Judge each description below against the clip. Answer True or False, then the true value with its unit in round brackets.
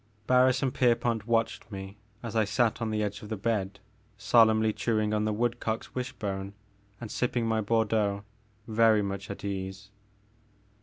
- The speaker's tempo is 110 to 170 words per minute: True (165 wpm)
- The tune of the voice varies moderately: False (2.3 semitones)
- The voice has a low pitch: True (110 Hz)